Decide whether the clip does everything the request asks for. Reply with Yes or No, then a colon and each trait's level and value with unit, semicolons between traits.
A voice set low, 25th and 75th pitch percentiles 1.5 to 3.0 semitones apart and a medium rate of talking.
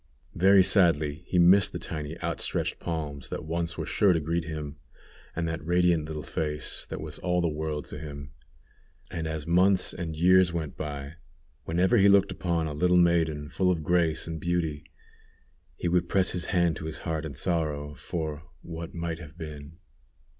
Yes: very low, 80 Hz; narrow, 2.4 semitones; average, 180 wpm